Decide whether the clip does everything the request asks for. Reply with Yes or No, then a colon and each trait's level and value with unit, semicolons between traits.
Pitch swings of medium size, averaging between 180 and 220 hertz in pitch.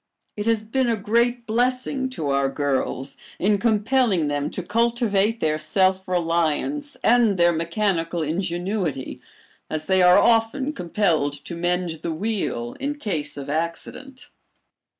No: wide, 6.0 semitones; high, 190 Hz